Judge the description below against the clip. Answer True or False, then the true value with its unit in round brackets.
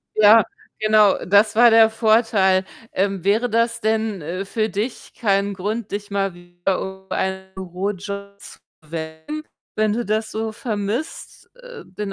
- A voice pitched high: True (205 Hz)